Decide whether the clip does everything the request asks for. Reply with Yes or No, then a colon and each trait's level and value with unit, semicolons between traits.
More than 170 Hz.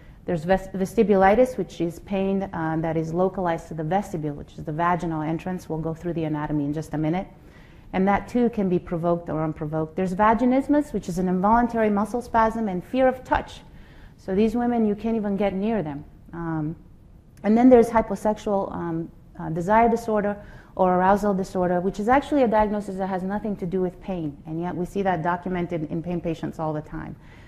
Yes: medium, 185 Hz